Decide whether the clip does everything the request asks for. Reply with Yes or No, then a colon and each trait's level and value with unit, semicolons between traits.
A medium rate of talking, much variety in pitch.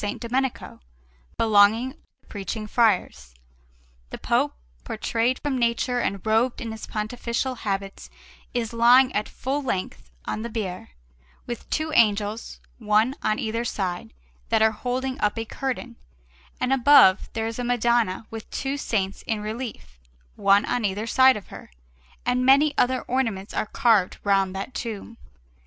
No: average, 150 wpm; average, 3.2 semitones